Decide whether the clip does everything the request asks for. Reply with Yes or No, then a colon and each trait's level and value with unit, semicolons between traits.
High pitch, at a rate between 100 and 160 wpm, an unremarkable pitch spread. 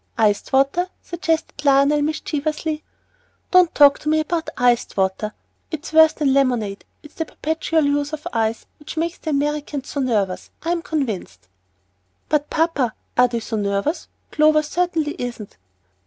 Yes: very high, 295 Hz; average, 150 wpm; average, 4.4 semitones